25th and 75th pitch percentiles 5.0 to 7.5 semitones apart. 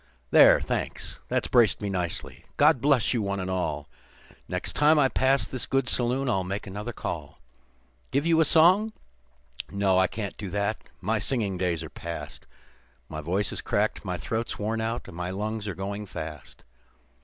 Yes: average, 5.3 semitones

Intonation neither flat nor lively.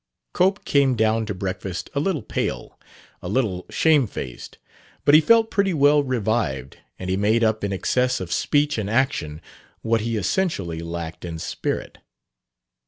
No: wide, 7.4 semitones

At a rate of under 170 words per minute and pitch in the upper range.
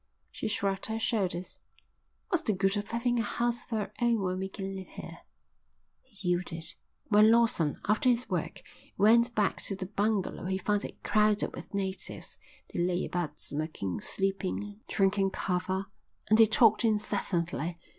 Yes: average, 160 wpm; high, 200 Hz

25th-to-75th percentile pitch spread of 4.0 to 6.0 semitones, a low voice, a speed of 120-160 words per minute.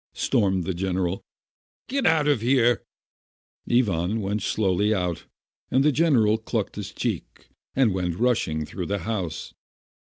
Yes: average, 5.2 semitones; low, 105 Hz; average, 145 wpm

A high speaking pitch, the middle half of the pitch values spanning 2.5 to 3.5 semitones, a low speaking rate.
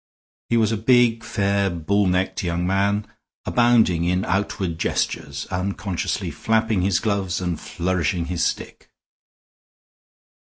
No: very low, 95 Hz; average, 2.8 semitones; slow, 120 wpm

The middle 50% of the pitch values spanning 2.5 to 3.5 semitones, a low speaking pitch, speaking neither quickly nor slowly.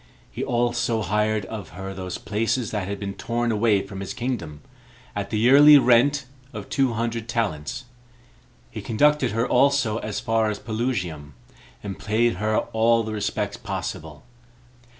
Yes: average, 3.0 semitones; low, 110 Hz; average, 150 wpm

